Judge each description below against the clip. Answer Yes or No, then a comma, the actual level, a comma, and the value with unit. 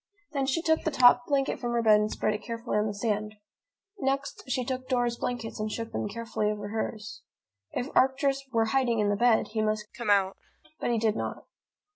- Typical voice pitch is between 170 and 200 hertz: No, high, 230 Hz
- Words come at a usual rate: No, fast, 210 wpm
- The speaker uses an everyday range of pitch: Yes, average, 3.3 semitones